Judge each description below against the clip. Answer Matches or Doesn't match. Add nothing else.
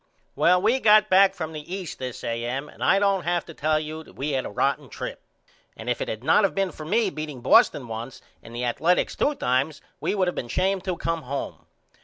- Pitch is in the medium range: Matches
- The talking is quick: Matches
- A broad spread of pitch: Matches